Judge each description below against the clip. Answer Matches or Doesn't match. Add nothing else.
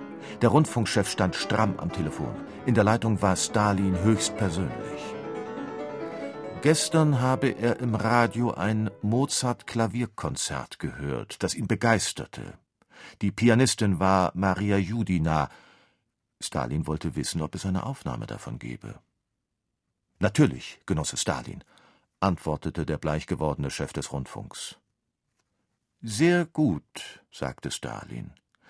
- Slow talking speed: Matches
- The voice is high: Doesn't match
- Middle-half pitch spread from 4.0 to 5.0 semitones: Matches